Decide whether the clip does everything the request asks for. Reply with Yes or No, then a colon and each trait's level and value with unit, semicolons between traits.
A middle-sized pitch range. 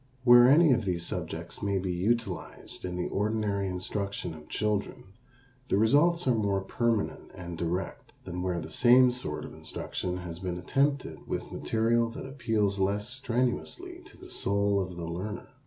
Yes: average, 4.9 semitones